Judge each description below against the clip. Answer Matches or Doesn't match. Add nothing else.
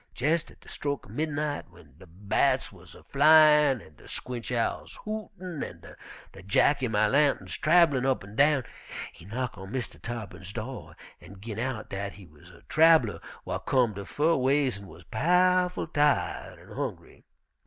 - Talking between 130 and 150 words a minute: Doesn't match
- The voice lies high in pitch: Doesn't match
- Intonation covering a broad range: Matches